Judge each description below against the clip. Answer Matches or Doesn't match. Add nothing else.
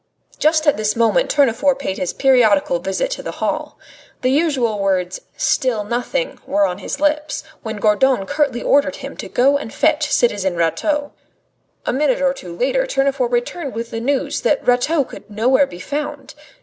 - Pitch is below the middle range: Doesn't match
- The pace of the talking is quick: Doesn't match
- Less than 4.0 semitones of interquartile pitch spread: Doesn't match